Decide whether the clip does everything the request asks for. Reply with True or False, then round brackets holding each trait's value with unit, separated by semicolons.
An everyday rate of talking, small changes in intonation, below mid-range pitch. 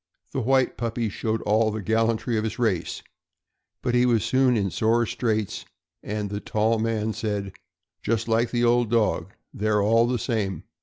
True (170 wpm; 1.9 semitones; 110 Hz)